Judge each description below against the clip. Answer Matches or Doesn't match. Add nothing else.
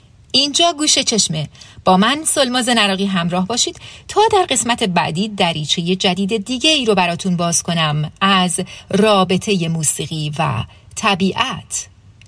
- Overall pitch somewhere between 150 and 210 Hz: Matches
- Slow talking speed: Matches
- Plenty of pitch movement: Matches